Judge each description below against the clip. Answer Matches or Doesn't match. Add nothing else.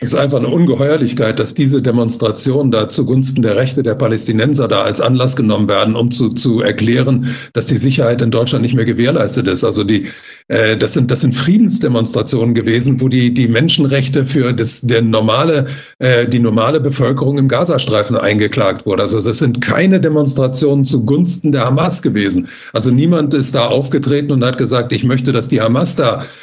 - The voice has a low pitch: Matches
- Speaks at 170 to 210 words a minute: Matches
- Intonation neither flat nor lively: Matches